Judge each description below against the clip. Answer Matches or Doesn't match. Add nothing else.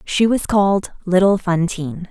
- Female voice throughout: Matches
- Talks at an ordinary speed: Matches